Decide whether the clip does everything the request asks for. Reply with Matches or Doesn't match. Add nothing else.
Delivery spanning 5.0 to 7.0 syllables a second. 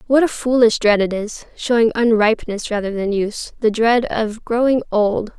Doesn't match